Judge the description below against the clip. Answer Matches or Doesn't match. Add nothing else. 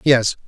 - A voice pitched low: Matches